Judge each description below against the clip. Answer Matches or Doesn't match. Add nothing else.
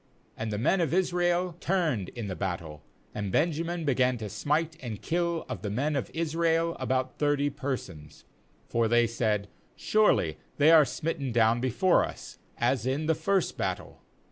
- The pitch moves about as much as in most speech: Doesn't match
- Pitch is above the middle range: Doesn't match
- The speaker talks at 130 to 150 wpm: Doesn't match